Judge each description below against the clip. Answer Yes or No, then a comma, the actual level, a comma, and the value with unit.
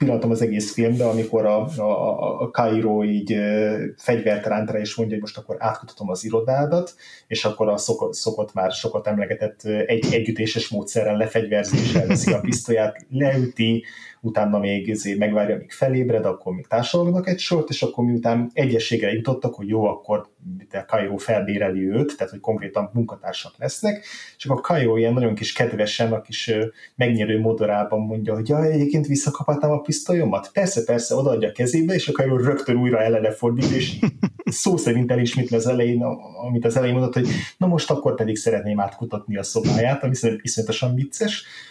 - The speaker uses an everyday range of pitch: Yes, average, 3.6 semitones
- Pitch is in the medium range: No, low, 115 Hz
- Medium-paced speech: No, fast, 170 wpm